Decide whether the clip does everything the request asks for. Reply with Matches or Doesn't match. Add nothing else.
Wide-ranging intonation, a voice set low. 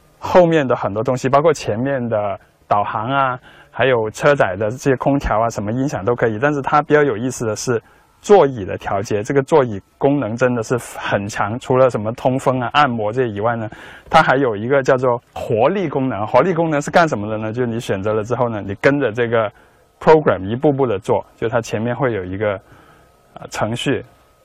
Doesn't match